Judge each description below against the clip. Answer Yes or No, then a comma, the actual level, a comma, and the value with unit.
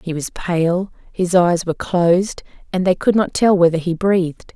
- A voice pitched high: No, medium, 175 Hz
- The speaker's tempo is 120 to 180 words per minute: No, average, 200 wpm